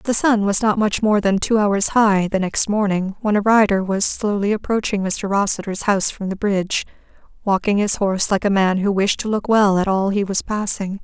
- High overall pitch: Yes, high, 200 Hz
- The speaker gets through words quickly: Yes, fast, 225 wpm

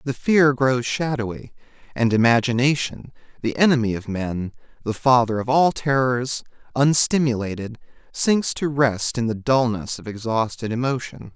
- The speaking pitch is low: Yes, low, 125 Hz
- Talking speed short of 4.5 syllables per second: No, 4.6 syllables/s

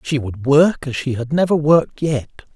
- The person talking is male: Yes, male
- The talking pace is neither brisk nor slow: No, fast, 210 wpm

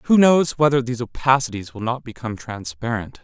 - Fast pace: No, average, 165 wpm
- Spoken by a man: Yes, male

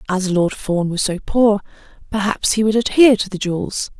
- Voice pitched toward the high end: Yes, high, 205 Hz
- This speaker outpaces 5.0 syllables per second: Yes, 5.3 syllables/s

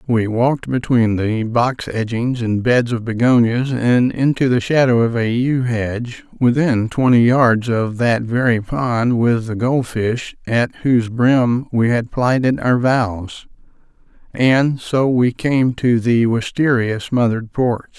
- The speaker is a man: Yes, male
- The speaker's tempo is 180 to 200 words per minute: No, average, 155 wpm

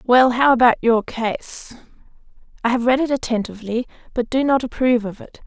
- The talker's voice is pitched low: No, high, 240 Hz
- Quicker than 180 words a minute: No, average, 175 wpm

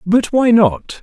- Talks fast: No, average, 175 wpm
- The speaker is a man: Yes, male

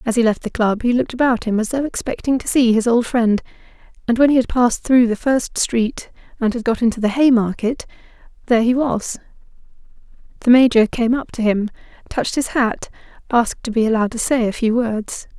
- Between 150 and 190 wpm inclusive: No, fast, 205 wpm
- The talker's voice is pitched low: No, high, 235 Hz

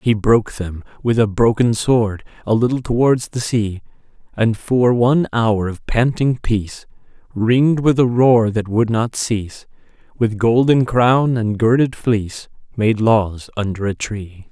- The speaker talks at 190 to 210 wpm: No, average, 155 wpm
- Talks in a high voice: No, low, 115 Hz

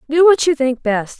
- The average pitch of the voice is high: Yes, very high, 290 Hz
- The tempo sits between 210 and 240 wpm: No, fast, 250 wpm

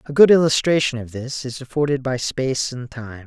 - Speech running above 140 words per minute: Yes, average, 200 wpm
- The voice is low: Yes, low, 130 Hz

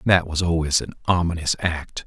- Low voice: Yes, very low, 85 Hz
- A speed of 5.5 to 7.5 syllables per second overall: No, 4.9 syllables/s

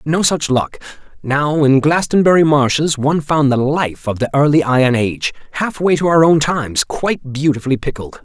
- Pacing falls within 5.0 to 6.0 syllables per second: Yes, 5.3 syllables/s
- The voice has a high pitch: No, medium, 145 Hz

